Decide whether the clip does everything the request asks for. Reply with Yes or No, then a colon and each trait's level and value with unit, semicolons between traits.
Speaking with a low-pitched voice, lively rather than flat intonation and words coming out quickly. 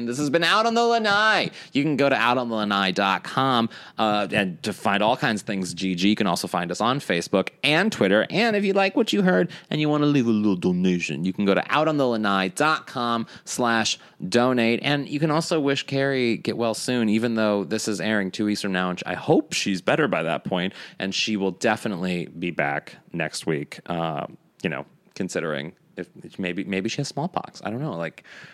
Yes: low, 115 Hz; wide, 6.6 semitones; fast, 210 wpm